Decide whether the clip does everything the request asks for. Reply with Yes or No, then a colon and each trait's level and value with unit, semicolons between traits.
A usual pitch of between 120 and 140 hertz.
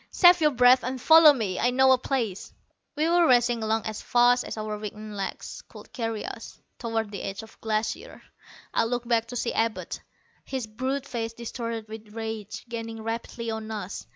No: high, 230 Hz